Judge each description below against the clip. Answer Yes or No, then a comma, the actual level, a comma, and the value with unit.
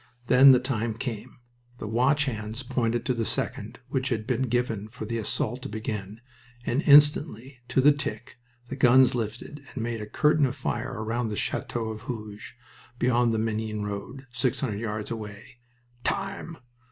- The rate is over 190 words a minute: No, average, 170 wpm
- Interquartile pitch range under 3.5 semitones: Yes, average, 3.1 semitones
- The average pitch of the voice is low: Yes, low, 120 Hz